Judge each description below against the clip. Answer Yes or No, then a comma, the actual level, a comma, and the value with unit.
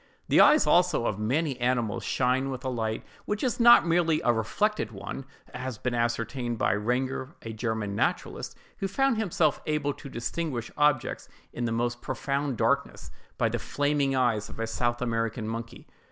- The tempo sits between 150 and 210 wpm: Yes, average, 170 wpm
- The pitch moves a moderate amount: Yes, average, 4.2 semitones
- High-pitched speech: No, low, 125 Hz